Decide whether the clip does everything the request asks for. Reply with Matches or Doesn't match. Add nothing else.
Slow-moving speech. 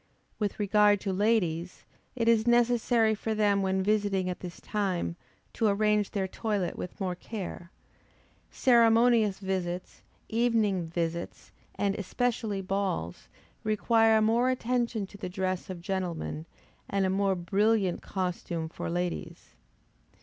Matches